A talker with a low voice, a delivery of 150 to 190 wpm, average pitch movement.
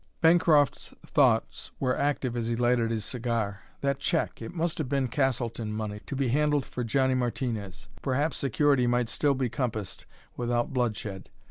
Yes: low, 125 Hz; average, 160 wpm; average, 3.3 semitones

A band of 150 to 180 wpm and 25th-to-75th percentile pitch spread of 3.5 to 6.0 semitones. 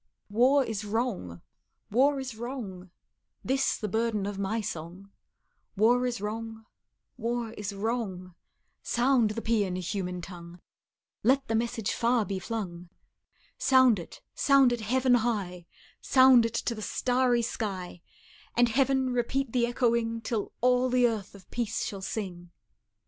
No: average, 140 wpm; average, 3.8 semitones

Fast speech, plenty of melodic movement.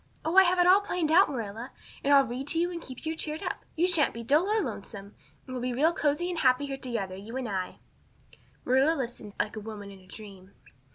Yes: fast, 245 wpm; wide, 6.7 semitones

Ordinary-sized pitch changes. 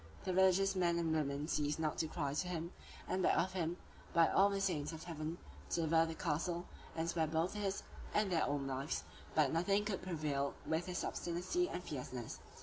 Yes: average, 3.1 semitones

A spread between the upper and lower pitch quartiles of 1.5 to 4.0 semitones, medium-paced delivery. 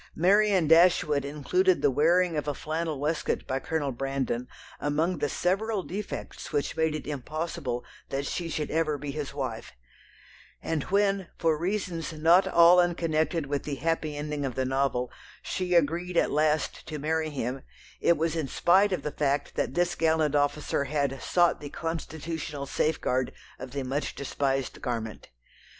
Yes: average, 3.1 semitones; average, 160 wpm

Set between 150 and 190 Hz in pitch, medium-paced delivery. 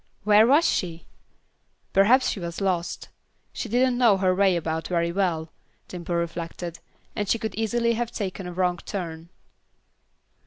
Yes: medium, 185 Hz; average, 150 wpm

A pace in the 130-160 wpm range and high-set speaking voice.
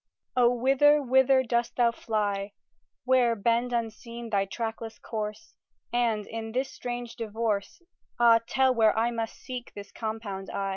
Yes: average, 145 wpm; high, 230 Hz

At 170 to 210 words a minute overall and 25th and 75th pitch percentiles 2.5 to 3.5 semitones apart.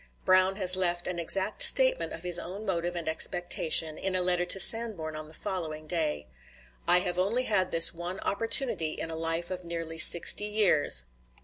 Yes: average, 185 wpm; average, 2.8 semitones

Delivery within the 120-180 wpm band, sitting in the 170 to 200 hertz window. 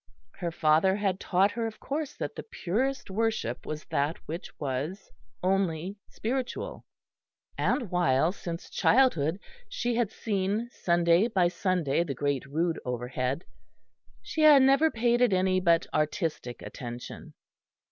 Yes: slow, 135 wpm; medium, 185 Hz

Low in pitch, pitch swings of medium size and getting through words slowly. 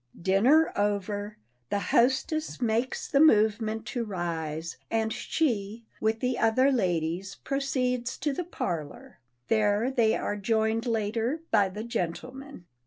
No: high, 220 Hz; average, 3.9 semitones; slow, 125 wpm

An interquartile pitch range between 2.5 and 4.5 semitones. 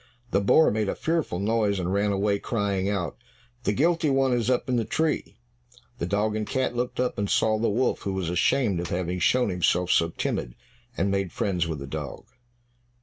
No: average, 5.1 semitones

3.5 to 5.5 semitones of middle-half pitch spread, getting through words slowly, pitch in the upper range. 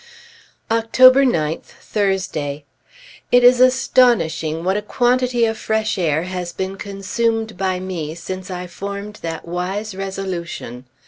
Yes: average, 4.5 semitones; slow, 125 wpm; high, 195 Hz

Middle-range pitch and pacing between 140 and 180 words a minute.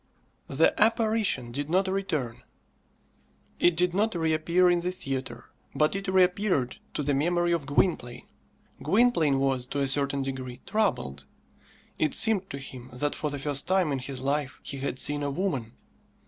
Yes: medium, 150 Hz; average, 160 wpm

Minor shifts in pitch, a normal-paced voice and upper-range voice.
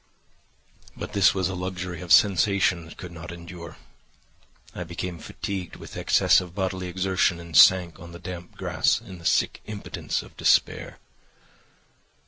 No: narrow, 1.6 semitones; average, 150 wpm; very low, 90 Hz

